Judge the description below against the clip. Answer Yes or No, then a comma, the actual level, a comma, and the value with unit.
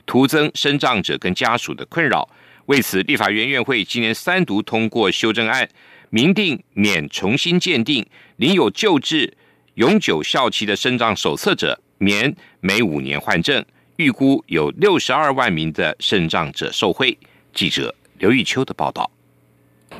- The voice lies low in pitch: Yes, low, 125 Hz